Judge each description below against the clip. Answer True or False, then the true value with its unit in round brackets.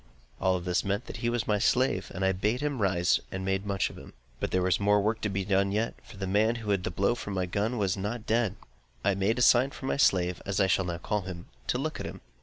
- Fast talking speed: True (280 wpm)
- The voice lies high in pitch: False (100 Hz)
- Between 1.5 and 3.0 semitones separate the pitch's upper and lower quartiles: True (2.7 semitones)